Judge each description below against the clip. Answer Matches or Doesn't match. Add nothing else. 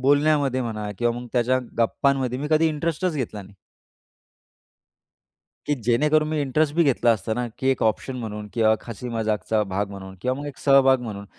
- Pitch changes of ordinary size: Matches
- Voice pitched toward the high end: Doesn't match